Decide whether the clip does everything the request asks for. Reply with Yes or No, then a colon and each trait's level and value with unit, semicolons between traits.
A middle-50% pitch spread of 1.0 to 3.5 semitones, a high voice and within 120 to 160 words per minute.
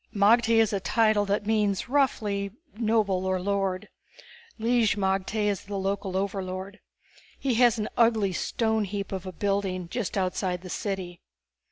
Yes: narrow, 2.5 semitones; high, 200 Hz; average, 145 wpm